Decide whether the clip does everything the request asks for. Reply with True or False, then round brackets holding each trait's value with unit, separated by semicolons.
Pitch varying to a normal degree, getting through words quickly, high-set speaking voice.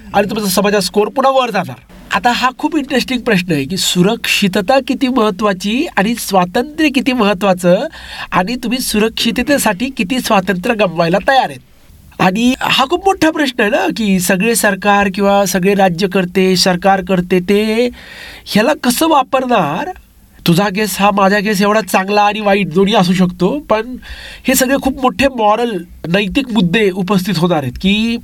True (4.3 semitones; 155 wpm; 210 Hz)